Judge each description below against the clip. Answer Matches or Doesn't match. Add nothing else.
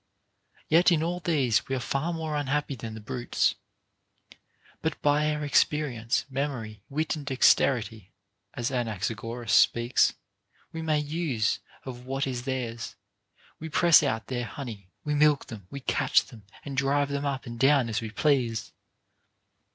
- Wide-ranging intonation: Doesn't match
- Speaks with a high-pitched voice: Doesn't match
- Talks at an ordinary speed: Matches